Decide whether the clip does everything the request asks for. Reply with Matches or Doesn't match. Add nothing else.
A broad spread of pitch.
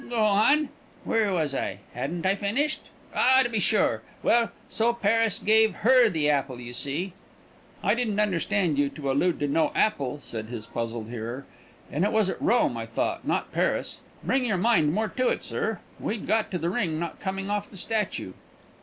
Matches